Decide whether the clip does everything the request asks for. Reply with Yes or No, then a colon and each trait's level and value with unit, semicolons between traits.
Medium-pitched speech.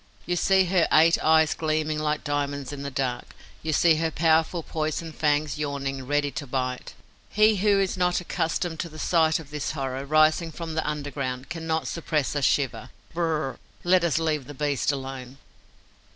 Yes: medium, 155 Hz